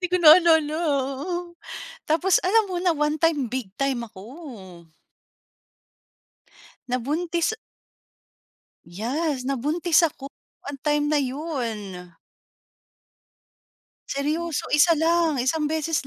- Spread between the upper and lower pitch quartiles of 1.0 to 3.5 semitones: No, average, 4.2 semitones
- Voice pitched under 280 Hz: No, very high, 300 Hz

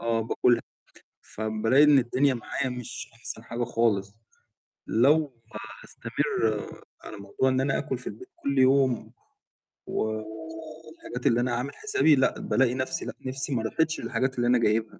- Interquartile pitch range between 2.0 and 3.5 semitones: Yes, average, 3.0 semitones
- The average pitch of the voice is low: Yes, low, 125 Hz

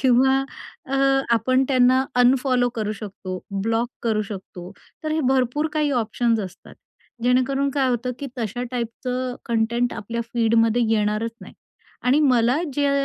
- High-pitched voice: Yes, high, 245 Hz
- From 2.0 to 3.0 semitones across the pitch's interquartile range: Yes, narrow, 2.4 semitones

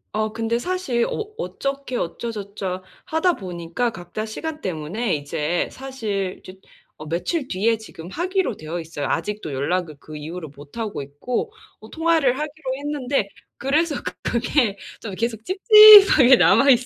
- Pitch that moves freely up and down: Yes, wide, 8.2 semitones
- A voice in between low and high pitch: No, high, 225 Hz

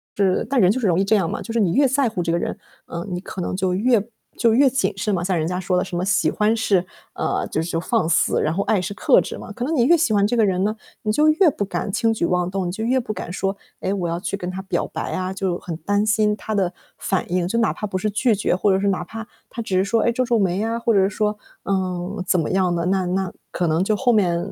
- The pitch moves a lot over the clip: No, average, 3.4 semitones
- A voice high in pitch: Yes, high, 195 Hz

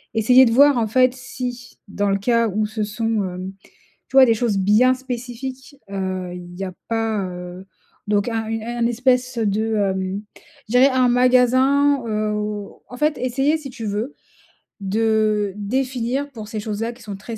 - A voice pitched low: No, high, 225 Hz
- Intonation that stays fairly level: No, average, 3.5 semitones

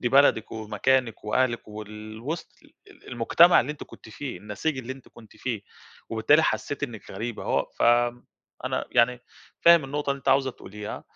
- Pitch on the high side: No, low, 120 Hz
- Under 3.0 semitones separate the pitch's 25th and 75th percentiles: No, average, 4.1 semitones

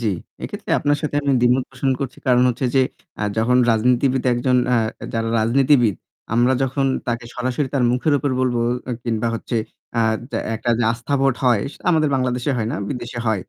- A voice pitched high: No, low, 125 Hz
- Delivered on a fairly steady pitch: Yes, narrow, 2.1 semitones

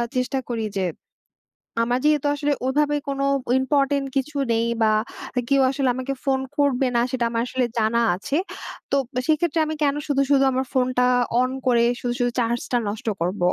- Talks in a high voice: Yes, very high, 260 Hz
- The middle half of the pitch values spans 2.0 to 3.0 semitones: Yes, average, 2.7 semitones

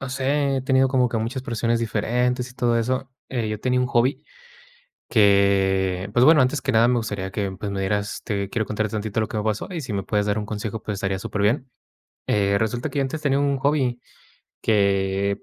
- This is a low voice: Yes, low, 110 Hz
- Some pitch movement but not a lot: Yes, average, 4.1 semitones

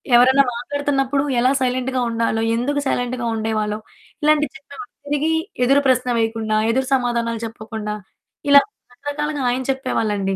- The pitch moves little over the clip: No, average, 3.5 semitones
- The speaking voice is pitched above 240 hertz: Yes, very high, 250 Hz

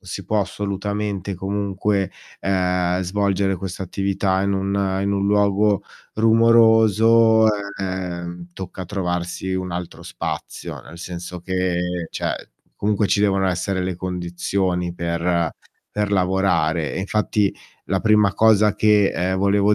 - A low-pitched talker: Yes, very low, 95 Hz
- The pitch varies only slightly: Yes, narrow, 2.2 semitones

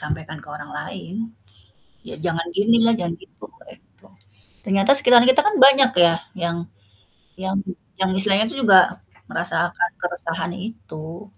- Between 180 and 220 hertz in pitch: Yes, medium, 185 Hz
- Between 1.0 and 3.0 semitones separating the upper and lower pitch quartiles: No, average, 5.1 semitones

